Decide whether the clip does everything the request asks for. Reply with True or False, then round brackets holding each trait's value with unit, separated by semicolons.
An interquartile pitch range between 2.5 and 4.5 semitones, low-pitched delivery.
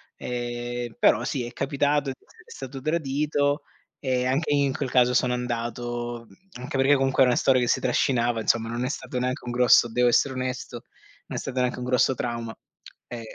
False (1.9 semitones; 125 Hz)